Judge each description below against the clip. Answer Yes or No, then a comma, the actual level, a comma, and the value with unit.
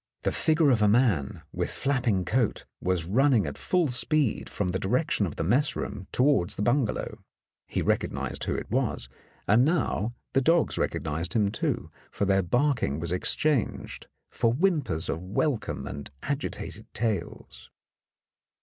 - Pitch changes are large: Yes, wide, 7.1 semitones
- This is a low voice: Yes, low, 115 Hz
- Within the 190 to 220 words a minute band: No, average, 155 wpm